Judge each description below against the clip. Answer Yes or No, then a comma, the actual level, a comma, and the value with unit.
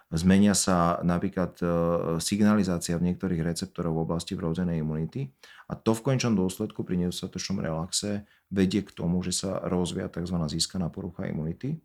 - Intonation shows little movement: No, average, 3.2 semitones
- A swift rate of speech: No, average, 145 wpm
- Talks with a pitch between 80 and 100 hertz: Yes, very low, 90 Hz